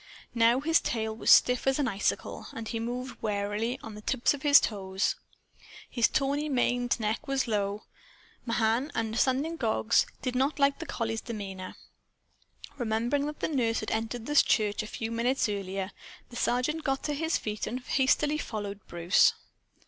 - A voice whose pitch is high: Yes, high, 235 Hz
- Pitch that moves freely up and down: No, average, 3.9 semitones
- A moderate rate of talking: Yes, average, 165 wpm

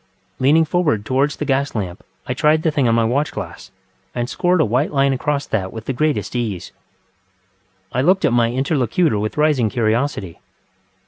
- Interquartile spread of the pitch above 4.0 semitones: Yes, average, 4.9 semitones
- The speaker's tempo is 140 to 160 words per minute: No, average, 180 wpm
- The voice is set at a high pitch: No, low, 130 Hz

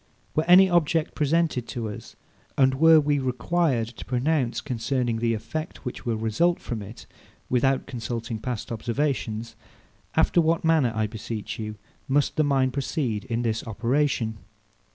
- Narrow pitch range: No, average, 4.8 semitones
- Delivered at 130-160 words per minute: Yes, average, 150 wpm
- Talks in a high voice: No, low, 125 Hz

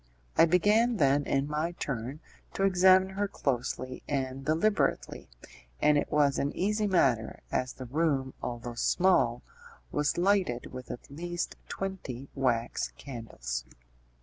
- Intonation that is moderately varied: No, wide, 6.3 semitones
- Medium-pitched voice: Yes, medium, 145 Hz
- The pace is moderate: No, slow, 130 wpm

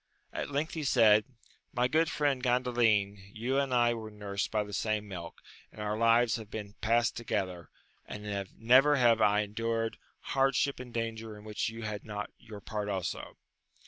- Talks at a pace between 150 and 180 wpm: Yes, average, 175 wpm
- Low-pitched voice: Yes, low, 110 Hz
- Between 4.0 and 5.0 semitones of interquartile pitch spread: No, average, 2.7 semitones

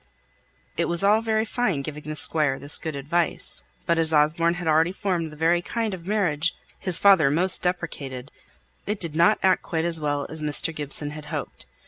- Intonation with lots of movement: No, average, 3.4 semitones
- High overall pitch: No, medium, 165 Hz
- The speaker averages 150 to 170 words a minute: No, average, 190 wpm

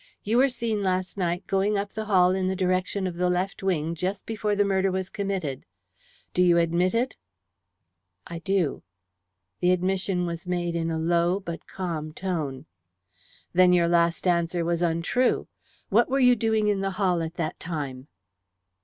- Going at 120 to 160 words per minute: No, average, 170 wpm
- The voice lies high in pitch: No, medium, 180 Hz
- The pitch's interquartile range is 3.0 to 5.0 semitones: No, narrow, 2.5 semitones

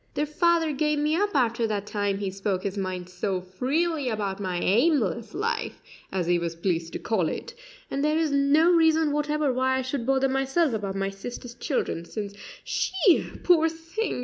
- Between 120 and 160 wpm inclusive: No, average, 185 wpm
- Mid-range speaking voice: No, very high, 260 Hz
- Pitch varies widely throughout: Yes, wide, 7.7 semitones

